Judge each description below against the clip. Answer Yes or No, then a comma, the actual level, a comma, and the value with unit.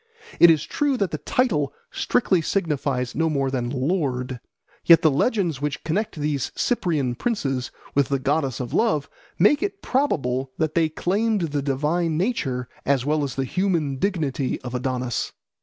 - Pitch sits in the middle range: Yes, medium, 150 Hz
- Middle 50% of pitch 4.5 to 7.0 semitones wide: Yes, average, 5.1 semitones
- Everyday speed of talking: Yes, average, 160 wpm